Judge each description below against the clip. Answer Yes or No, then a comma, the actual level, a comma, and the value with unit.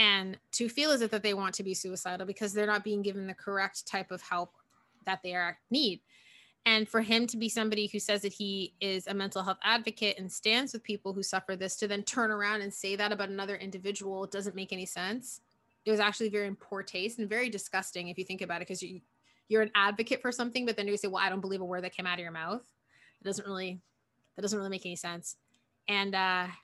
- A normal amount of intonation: No, narrow, 2.1 semitones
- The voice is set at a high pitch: Yes, high, 200 Hz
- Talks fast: Yes, fast, 250 wpm